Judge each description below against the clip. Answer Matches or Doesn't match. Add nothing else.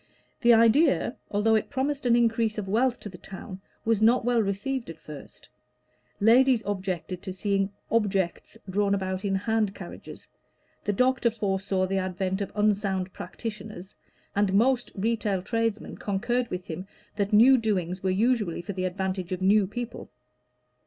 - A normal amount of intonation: Matches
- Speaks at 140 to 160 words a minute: Matches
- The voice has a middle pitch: Doesn't match